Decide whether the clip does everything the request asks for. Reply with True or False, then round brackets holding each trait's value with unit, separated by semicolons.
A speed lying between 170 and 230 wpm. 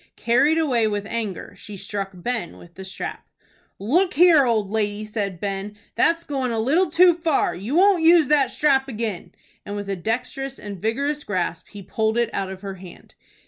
True (185 wpm)